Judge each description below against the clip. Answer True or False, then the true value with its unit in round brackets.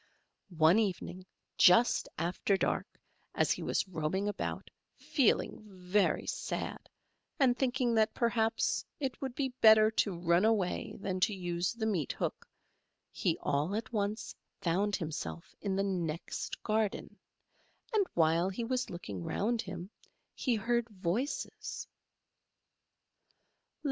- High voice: True (200 Hz)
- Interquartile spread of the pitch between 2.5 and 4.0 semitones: False (4.4 semitones)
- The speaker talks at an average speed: False (130 wpm)